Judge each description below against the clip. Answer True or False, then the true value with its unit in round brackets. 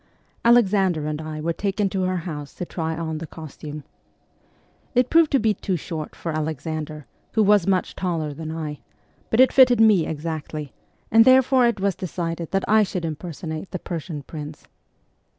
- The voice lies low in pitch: False (170 Hz)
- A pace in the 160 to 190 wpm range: True (170 wpm)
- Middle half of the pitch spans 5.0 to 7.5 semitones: False (4.5 semitones)